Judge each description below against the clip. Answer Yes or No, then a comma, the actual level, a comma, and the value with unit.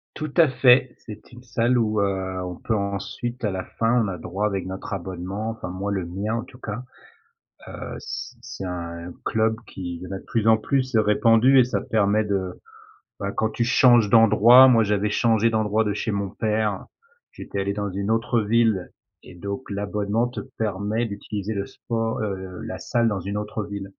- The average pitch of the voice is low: Yes, low, 105 Hz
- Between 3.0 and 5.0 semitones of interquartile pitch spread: No, narrow, 2.6 semitones